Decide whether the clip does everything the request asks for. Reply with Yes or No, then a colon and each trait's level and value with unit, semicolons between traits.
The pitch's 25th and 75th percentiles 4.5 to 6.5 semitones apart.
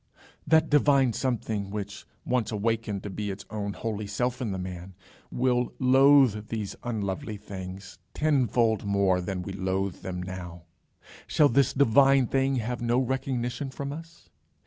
Yes: average, 4.9 semitones